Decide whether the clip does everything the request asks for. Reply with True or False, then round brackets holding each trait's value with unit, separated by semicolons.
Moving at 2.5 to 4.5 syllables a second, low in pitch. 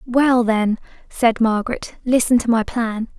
False (4.2 syllables/s; 235 Hz)